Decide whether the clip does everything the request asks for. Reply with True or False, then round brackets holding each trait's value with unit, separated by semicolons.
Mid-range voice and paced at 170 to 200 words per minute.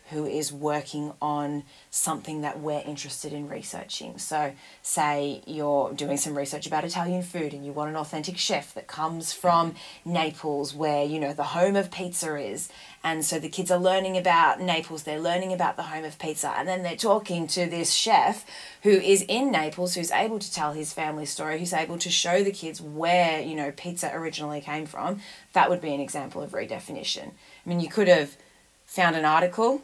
True (160 Hz; 195 wpm)